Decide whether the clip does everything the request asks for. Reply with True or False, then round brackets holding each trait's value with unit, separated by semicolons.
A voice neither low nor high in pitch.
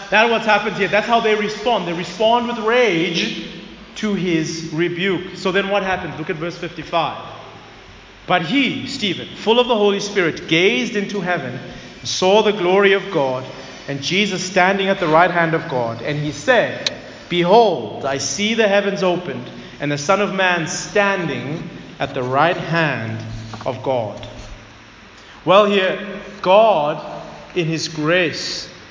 True (180 Hz)